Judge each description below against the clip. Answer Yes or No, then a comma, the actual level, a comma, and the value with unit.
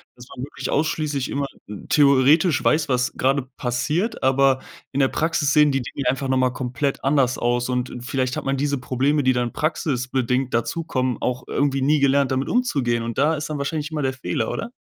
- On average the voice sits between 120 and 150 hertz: Yes, low, 135 Hz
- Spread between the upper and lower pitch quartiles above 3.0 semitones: No, narrow, 2.5 semitones